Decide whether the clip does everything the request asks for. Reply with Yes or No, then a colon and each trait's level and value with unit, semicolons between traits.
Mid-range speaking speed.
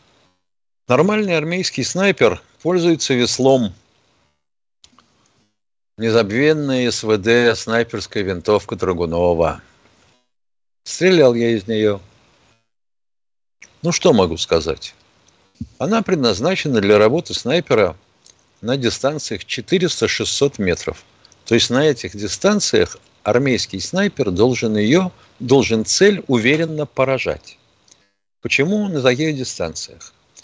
No: slow, 85 wpm